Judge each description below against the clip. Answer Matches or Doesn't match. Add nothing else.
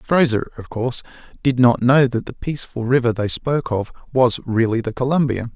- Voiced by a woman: Doesn't match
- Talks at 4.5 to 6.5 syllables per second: Matches